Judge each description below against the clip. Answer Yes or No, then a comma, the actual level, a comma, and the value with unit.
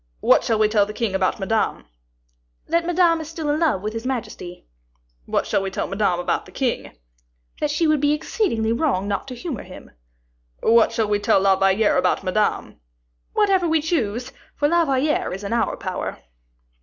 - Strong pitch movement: Yes, wide, 7.4 semitones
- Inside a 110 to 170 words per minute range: No, average, 190 wpm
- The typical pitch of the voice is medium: No, high, 230 Hz